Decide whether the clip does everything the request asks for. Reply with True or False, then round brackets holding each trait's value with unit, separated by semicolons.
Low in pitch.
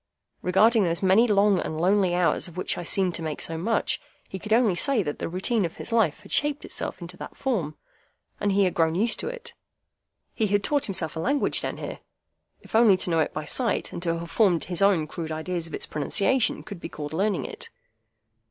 False (185 Hz)